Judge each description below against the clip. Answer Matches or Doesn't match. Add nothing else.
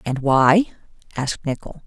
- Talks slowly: Matches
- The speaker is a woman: Matches